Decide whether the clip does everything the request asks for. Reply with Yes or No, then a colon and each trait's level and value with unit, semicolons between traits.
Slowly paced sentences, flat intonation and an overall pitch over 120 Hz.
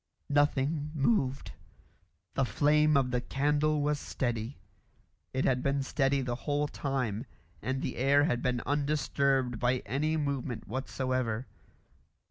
Yes: slow, 125 wpm; narrow, 2.3 semitones; low, 135 Hz